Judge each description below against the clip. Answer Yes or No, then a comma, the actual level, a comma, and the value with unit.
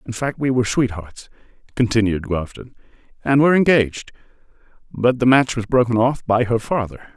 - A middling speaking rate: Yes, average, 160 wpm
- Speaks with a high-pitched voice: No, low, 120 Hz